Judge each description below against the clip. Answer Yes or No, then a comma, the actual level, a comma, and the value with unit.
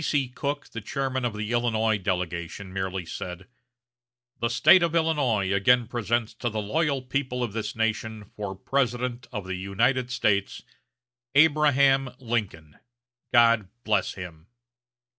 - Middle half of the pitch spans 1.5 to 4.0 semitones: No, average, 4.6 semitones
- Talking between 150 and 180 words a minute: No, slow, 135 wpm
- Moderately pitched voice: No, low, 115 Hz